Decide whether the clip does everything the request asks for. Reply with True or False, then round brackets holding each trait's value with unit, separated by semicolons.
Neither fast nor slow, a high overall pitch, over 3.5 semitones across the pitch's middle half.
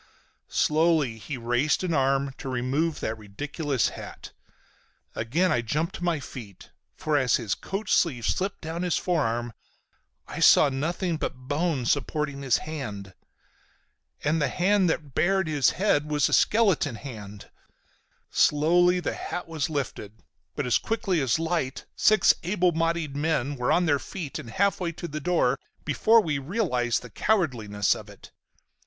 False (160 wpm; 150 Hz; 5.1 semitones)